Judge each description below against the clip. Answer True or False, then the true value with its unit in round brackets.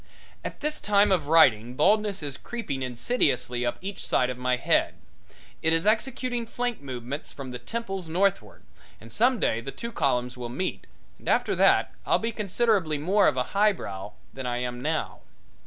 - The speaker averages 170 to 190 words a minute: True (175 wpm)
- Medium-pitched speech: True (160 Hz)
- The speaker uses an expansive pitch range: True (9.0 semitones)